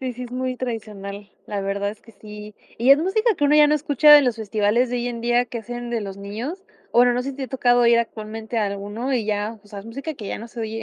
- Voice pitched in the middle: No, high, 235 Hz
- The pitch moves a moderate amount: Yes, average, 3.3 semitones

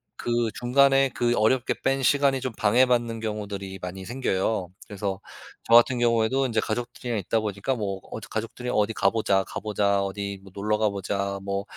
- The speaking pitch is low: Yes, low, 110 Hz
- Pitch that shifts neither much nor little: Yes, average, 3.6 semitones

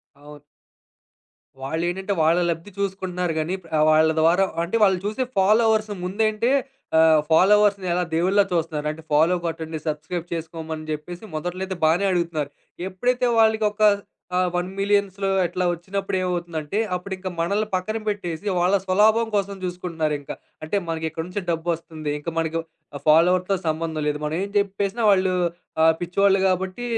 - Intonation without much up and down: No, average, 3.5 semitones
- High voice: No, medium, 180 Hz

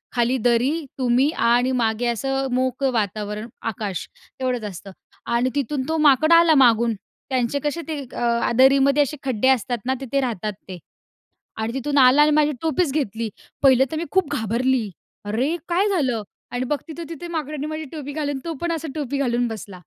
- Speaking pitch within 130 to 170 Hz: No, very high, 260 Hz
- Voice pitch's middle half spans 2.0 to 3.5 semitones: No, average, 4.1 semitones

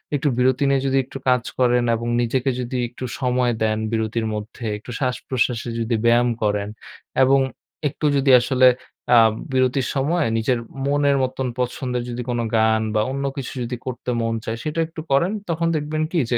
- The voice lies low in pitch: Yes, low, 125 Hz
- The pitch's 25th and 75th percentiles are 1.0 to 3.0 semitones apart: Yes, narrow, 2.6 semitones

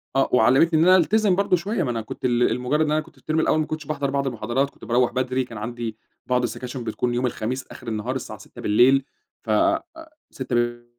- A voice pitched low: Yes, low, 130 Hz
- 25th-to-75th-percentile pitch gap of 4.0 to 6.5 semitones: Yes, average, 4.3 semitones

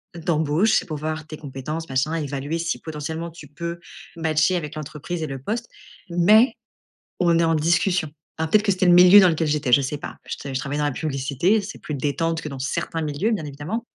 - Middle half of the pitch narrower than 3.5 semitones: Yes, average, 2.9 semitones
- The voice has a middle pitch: Yes, medium, 160 Hz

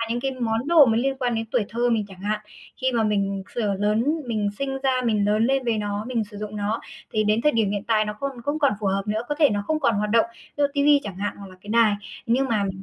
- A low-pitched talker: No, high, 225 Hz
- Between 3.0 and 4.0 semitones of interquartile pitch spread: Yes, average, 3.6 semitones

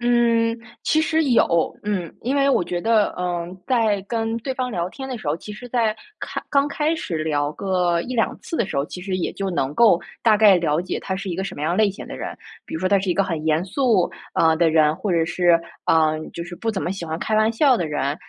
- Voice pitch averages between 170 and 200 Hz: Yes, high, 190 Hz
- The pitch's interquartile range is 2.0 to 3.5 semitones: No, average, 5.2 semitones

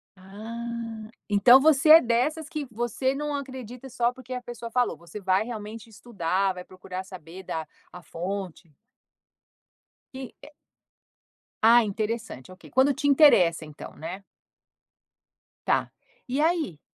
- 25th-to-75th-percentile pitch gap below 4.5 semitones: No, wide, 5.6 semitones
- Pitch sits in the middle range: No, high, 230 Hz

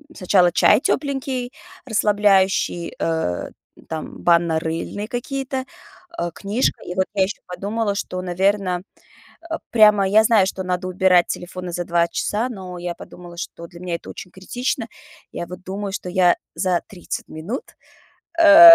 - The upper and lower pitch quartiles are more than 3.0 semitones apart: Yes, average, 3.5 semitones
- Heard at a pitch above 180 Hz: Yes, high, 190 Hz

